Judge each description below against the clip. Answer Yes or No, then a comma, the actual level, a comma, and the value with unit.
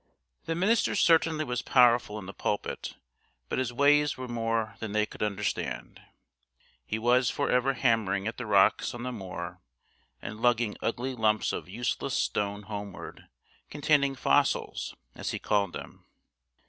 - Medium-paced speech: Yes, average, 150 wpm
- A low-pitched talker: Yes, low, 115 Hz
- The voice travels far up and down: No, average, 3.7 semitones